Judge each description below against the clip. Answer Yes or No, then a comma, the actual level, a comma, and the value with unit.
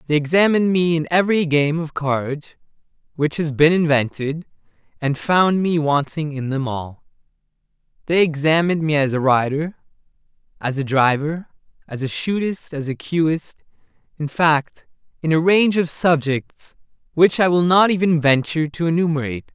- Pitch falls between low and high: Yes, medium, 155 Hz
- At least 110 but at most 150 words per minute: Yes, average, 145 wpm